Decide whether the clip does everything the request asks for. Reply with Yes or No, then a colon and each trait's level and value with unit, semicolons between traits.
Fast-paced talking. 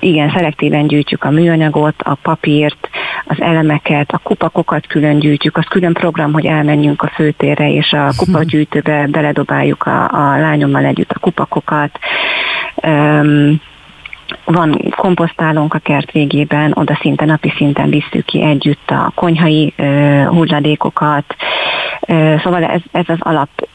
No: average, 135 wpm